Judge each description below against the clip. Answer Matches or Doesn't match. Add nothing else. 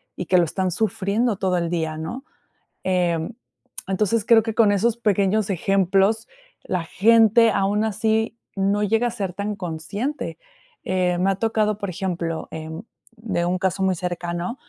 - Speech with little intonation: Doesn't match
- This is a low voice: Doesn't match